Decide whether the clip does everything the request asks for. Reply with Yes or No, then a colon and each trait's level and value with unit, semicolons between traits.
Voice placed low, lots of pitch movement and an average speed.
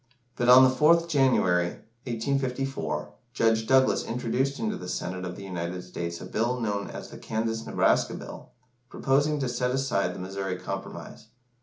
Yes: low, 120 Hz; wide, 5.7 semitones; average, 160 wpm